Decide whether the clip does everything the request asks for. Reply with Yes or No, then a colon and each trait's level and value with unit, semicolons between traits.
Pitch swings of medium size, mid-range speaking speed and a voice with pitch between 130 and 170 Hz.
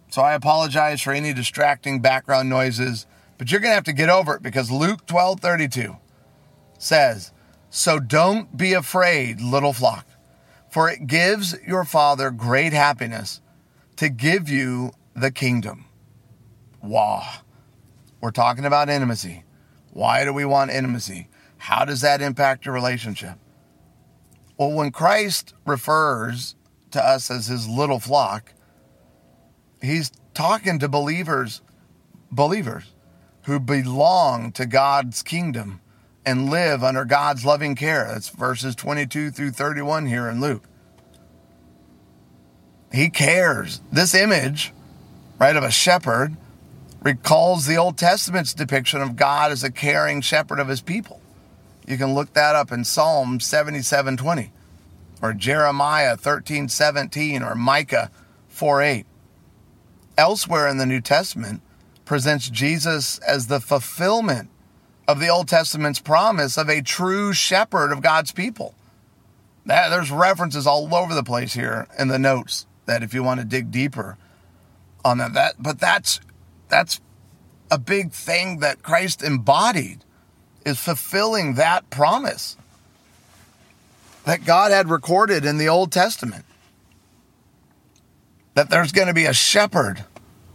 No: average, 4.3 semitones; slow, 130 wpm; medium, 140 Hz